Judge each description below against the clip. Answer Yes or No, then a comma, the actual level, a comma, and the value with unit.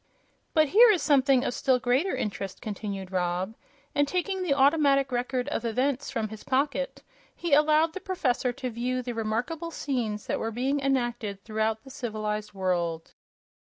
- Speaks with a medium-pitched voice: No, very high, 250 Hz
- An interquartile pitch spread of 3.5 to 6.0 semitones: Yes, average, 4.8 semitones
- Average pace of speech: Yes, average, 165 wpm